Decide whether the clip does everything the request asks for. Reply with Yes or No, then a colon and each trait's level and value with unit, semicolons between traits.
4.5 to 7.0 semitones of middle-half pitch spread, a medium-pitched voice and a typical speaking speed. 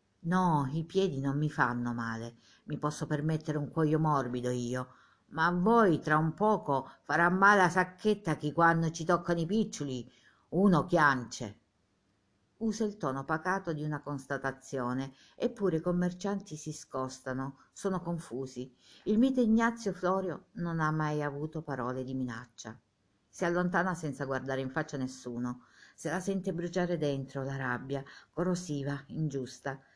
Yes: average, 5.2 semitones; medium, 150 Hz; average, 150 wpm